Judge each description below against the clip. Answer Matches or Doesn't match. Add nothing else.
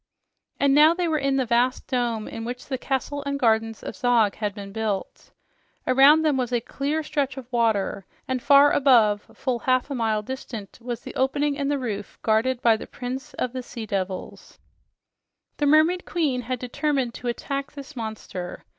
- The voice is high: Matches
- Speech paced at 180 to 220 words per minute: Matches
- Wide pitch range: Doesn't match